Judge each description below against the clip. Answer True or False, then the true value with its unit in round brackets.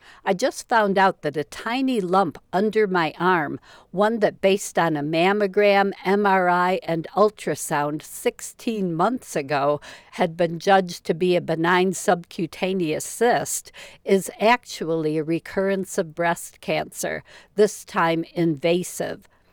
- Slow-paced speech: True (130 wpm)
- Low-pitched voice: False (185 Hz)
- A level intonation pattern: False (3.5 semitones)